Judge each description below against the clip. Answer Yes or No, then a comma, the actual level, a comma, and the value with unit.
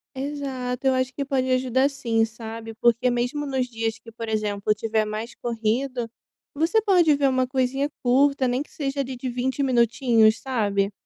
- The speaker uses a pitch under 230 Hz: No, very high, 250 Hz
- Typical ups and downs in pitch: Yes, average, 3.1 semitones